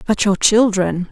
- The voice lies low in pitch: No, high, 205 Hz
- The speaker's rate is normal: Yes, average, 160 wpm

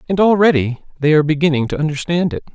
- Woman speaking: No, male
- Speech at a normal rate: Yes, average, 190 wpm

